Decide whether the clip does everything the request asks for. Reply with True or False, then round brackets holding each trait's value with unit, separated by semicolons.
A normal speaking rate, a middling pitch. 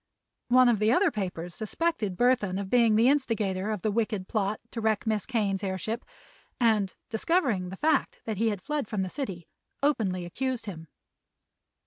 False (170 wpm; 215 Hz)